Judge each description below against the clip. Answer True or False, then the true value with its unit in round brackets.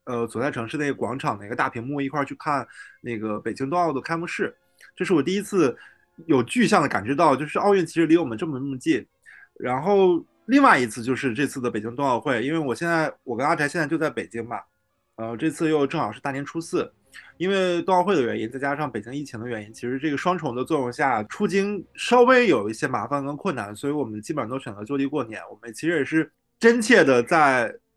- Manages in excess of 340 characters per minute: True (350 characters per minute)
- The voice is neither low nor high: True (145 Hz)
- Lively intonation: True (5.7 semitones)